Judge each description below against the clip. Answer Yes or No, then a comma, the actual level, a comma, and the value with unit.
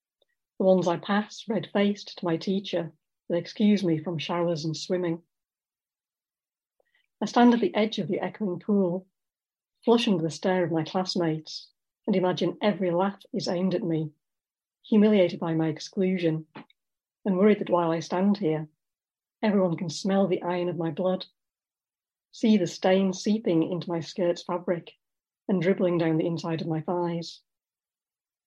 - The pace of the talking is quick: No, average, 155 wpm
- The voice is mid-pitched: Yes, medium, 180 Hz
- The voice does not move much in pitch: No, average, 3.1 semitones